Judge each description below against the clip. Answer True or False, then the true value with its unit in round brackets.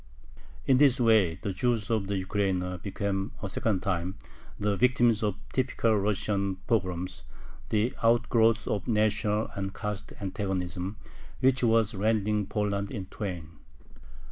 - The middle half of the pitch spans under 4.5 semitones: True (2.7 semitones)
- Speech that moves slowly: True (130 wpm)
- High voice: False (105 Hz)